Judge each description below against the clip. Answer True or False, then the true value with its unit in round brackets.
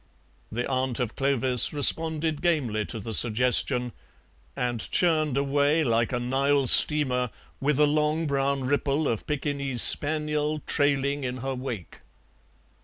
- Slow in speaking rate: True (130 wpm)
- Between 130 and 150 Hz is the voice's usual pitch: True (140 Hz)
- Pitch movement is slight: False (3.1 semitones)